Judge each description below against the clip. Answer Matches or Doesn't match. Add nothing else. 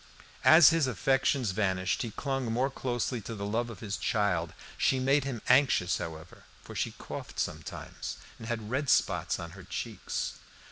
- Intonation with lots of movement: Matches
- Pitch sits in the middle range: Doesn't match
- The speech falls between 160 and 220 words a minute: Matches